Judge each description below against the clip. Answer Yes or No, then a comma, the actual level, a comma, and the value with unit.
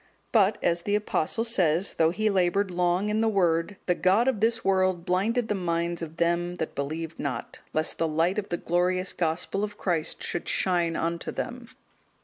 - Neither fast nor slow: Yes, average, 185 wpm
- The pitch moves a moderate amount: Yes, average, 3.4 semitones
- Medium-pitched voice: Yes, medium, 180 Hz